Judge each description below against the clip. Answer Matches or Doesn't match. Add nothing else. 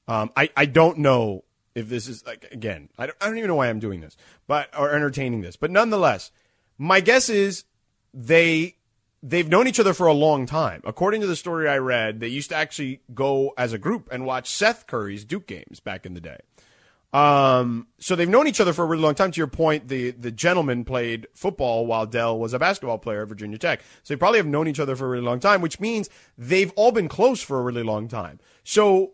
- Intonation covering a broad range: Matches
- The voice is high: Doesn't match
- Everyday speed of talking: Doesn't match